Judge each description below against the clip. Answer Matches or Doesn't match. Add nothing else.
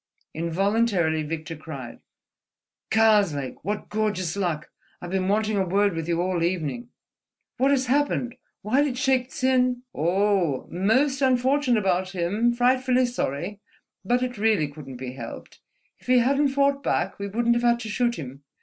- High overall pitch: Matches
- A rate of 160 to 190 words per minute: Doesn't match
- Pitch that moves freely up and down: Matches